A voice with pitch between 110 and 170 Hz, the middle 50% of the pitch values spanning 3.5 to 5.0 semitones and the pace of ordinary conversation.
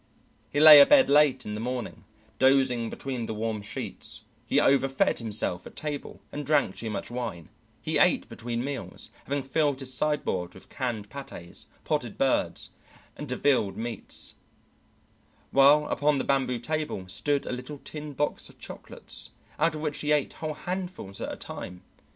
Yes: low, 135 Hz; average, 4.4 semitones; average, 160 wpm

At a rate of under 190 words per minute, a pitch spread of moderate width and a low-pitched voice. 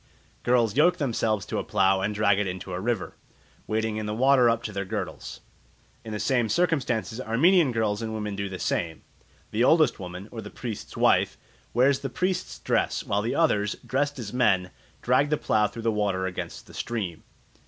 No: average, 195 wpm; average, 4.0 semitones; low, 110 Hz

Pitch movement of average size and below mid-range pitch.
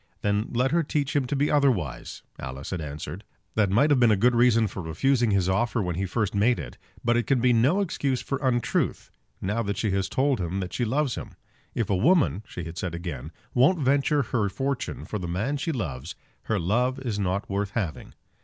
No: wide, 6.0 semitones; low, 115 Hz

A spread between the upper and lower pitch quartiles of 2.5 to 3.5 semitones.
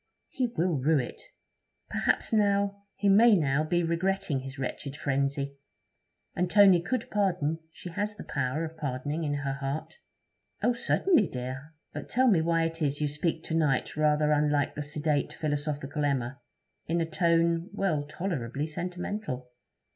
No: average, 4.1 semitones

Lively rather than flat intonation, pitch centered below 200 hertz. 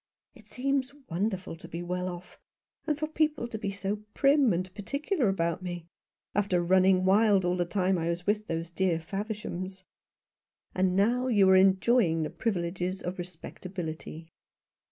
No: average, 3.4 semitones; high, 190 Hz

